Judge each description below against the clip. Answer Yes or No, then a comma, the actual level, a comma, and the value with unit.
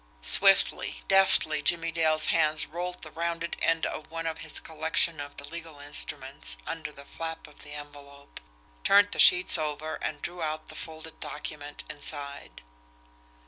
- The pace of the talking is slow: No, average, 155 wpm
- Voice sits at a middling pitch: Yes, medium, 155 Hz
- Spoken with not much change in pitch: Yes, narrow, 2.0 semitones